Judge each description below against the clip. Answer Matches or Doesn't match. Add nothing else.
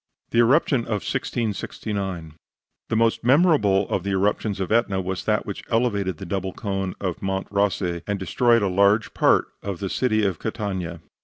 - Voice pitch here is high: Doesn't match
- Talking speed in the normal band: Matches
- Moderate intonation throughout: Matches